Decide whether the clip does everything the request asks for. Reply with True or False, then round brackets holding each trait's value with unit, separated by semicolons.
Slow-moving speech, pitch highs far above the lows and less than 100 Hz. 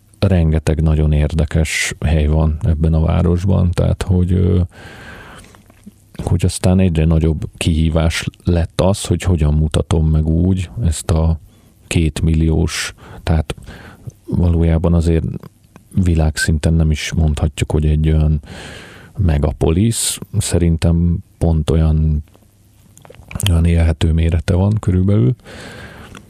False (100 wpm; 3.2 semitones; 85 Hz)